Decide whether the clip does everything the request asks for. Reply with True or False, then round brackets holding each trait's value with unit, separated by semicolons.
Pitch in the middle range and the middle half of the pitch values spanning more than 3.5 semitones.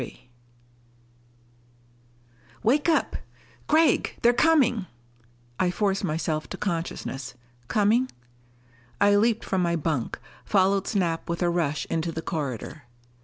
True (180 Hz; 5.4 semitones)